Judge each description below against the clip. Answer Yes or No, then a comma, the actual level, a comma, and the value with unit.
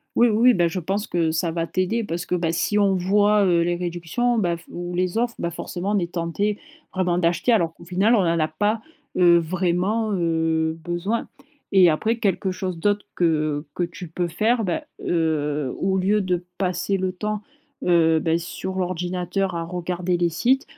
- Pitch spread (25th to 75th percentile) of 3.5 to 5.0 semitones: No, average, 2.9 semitones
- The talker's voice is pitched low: No, medium, 180 Hz